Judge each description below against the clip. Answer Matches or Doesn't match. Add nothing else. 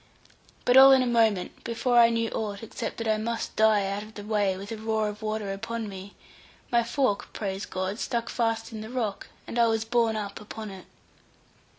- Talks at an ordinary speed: Doesn't match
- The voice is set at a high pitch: Matches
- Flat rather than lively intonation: Matches